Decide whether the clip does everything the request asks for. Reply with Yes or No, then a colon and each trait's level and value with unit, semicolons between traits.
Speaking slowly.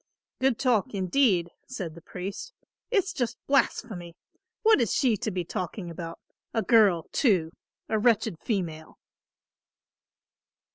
Yes: slow, 125 wpm